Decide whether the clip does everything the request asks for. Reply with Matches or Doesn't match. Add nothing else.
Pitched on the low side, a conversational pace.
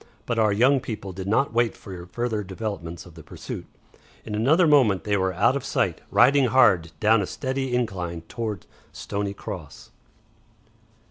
Matches